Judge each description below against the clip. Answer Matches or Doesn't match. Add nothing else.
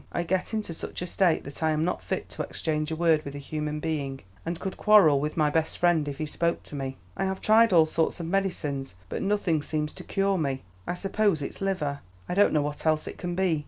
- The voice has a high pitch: Doesn't match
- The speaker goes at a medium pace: Doesn't match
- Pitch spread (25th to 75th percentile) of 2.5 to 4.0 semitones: Matches